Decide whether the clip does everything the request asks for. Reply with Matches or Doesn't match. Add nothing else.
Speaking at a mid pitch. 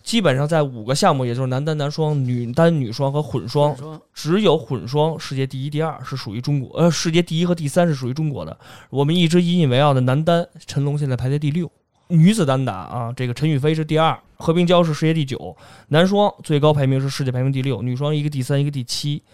Matches